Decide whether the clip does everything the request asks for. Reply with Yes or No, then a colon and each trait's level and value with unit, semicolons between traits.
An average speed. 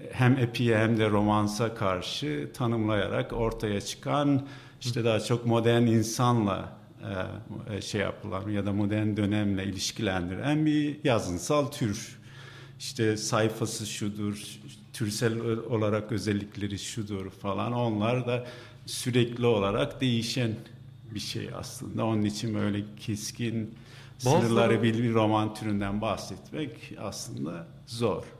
Yes: average, 110 wpm